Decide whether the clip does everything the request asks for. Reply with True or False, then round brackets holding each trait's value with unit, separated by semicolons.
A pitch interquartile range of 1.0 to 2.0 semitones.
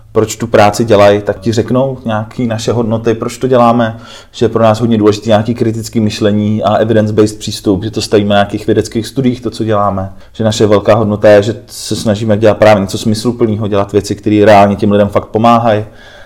True (1.5 semitones)